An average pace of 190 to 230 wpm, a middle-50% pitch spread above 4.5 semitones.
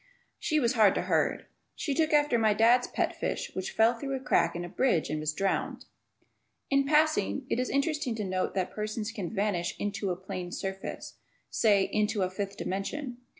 Yes: average, 195 wpm; average, 5.1 semitones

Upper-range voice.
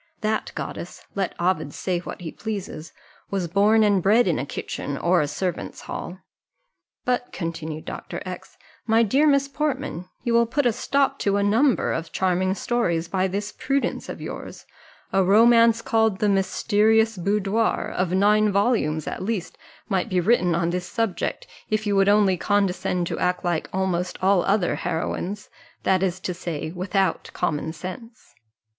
Yes: high, 195 Hz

